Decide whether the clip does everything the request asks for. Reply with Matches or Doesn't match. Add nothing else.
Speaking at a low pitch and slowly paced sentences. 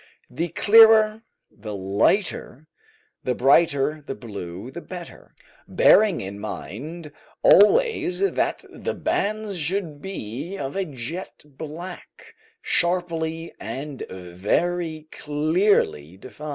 Doesn't match